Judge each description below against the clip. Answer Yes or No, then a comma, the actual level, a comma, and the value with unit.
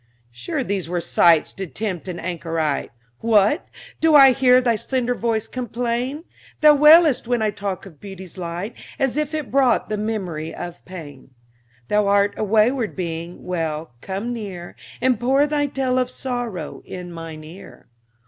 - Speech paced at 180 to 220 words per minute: No, average, 160 wpm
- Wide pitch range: Yes, wide, 6.3 semitones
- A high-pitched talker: Yes, high, 210 Hz